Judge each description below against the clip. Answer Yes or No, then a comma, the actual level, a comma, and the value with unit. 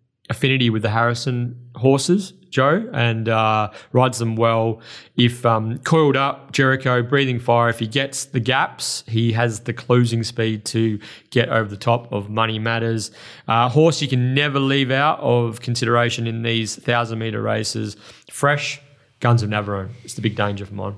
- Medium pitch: No, low, 120 Hz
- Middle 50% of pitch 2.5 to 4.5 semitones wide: Yes, average, 2.9 semitones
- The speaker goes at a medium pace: Yes, average, 170 wpm